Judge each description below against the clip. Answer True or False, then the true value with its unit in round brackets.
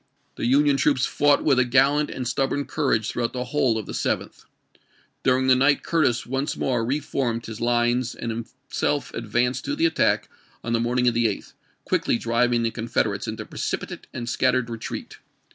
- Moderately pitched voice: False (125 Hz)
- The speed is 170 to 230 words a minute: True (180 wpm)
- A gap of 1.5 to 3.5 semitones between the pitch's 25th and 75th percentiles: True (2.7 semitones)